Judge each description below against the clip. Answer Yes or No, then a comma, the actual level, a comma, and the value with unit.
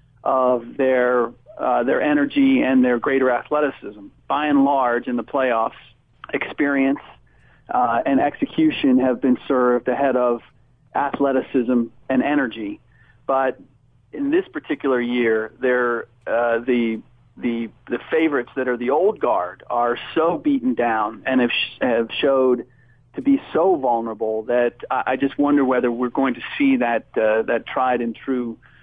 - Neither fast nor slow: Yes, average, 150 wpm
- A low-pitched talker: Yes, low, 125 Hz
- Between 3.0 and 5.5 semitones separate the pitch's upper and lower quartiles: No, narrow, 2.4 semitones